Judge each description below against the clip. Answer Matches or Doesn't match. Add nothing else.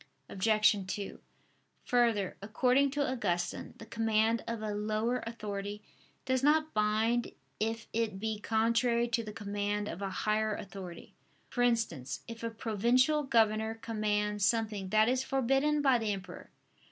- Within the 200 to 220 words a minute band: Doesn't match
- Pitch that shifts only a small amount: Matches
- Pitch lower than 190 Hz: Doesn't match